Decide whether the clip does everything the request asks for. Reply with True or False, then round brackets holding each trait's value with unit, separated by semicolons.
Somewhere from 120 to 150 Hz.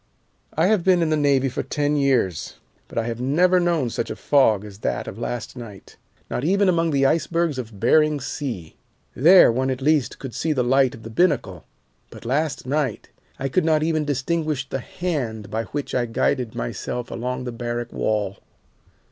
True (135 Hz)